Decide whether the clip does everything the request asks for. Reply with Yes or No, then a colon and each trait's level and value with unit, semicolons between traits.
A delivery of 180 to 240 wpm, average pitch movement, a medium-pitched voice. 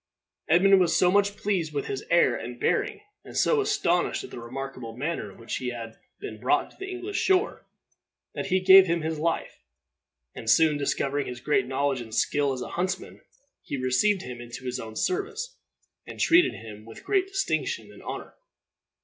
No: average, 185 wpm; wide, 8.4 semitones; medium, 160 Hz